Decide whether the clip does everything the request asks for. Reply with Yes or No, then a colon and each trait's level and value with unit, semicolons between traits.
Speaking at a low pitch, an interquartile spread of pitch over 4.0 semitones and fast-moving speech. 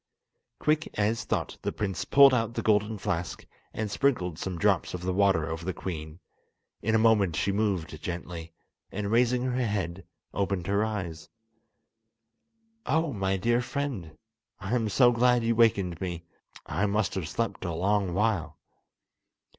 No: low, 100 Hz; average, 4.4 semitones; average, 155 wpm